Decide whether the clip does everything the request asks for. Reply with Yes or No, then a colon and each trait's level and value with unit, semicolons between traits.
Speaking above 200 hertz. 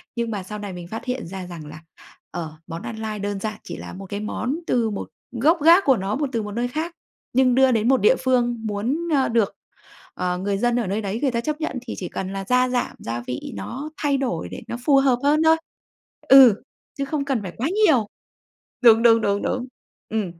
Yes: high, 230 Hz